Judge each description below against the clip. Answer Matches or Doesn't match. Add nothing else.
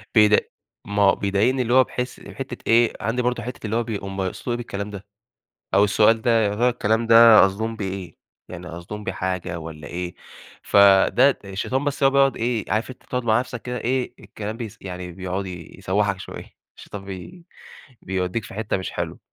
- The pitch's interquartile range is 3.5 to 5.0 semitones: Matches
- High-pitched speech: Doesn't match